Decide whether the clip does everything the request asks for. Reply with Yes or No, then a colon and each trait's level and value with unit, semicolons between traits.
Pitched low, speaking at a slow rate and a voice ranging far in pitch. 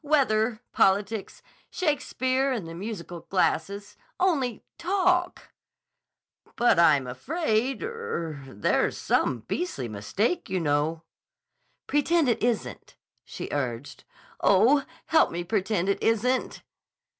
No: high, 215 Hz; slow, 100 wpm; wide, 8.5 semitones